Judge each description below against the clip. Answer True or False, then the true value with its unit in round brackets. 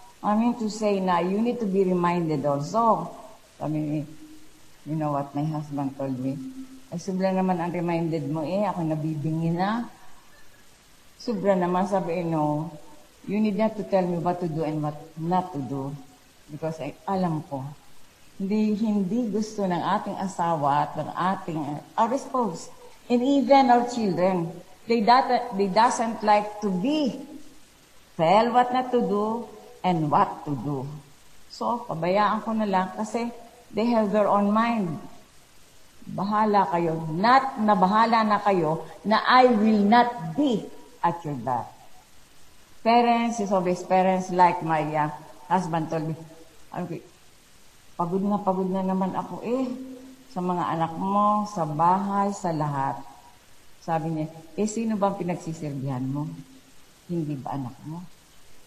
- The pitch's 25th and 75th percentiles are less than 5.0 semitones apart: False (5.4 semitones)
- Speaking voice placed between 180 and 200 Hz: True (185 Hz)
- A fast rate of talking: False (145 wpm)